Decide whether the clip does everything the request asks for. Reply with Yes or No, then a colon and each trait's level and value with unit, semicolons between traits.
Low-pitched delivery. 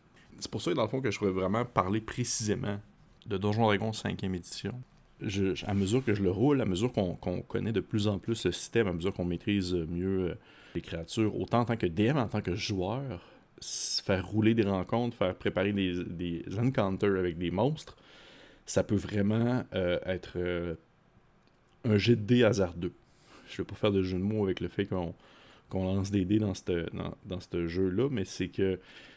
Yes: low, 100 Hz